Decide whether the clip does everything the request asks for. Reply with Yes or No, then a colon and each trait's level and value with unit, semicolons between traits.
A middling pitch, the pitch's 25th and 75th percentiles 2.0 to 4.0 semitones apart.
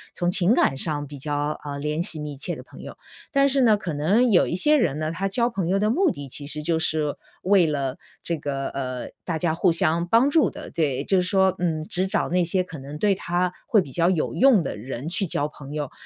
No: medium, 170 Hz; average, 4.7 semitones